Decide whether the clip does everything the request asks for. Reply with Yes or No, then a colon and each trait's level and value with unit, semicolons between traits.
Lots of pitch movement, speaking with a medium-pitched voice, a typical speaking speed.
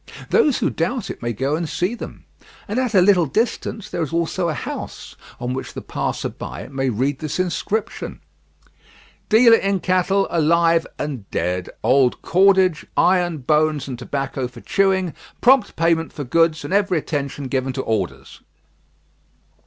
Yes: wide, 5.9 semitones; medium, 165 Hz; average, 160 wpm